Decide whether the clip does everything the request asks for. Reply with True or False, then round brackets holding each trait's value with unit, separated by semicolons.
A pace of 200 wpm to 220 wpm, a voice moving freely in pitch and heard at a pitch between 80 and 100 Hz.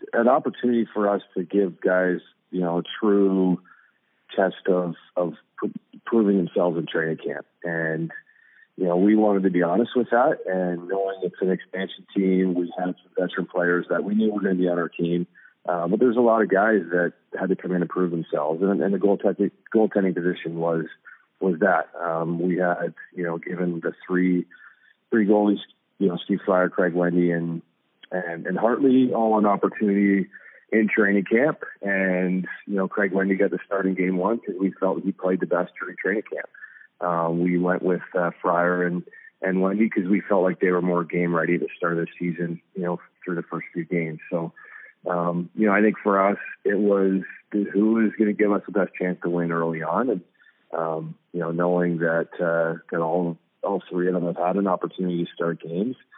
False (205 wpm; 2.4 semitones; 90 Hz)